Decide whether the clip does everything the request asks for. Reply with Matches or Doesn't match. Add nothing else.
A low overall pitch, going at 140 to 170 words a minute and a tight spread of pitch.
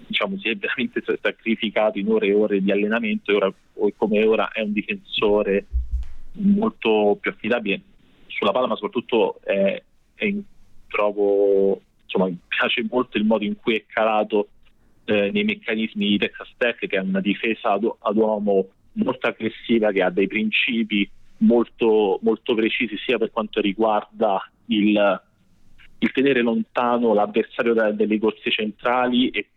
Matches